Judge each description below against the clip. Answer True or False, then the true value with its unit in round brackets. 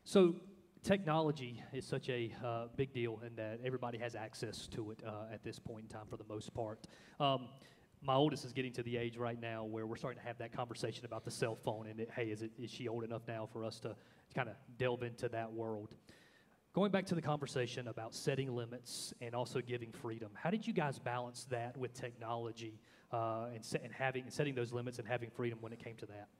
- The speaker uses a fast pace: True (230 wpm)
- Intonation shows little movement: True (2.2 semitones)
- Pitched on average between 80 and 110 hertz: False (120 Hz)